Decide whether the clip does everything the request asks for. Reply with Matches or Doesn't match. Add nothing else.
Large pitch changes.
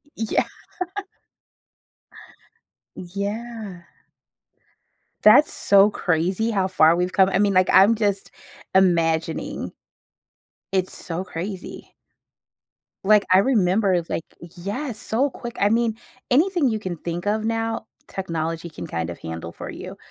Doesn't match